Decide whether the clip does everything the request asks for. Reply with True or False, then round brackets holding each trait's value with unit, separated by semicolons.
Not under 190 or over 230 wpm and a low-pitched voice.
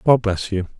True (225 wpm; 105 Hz)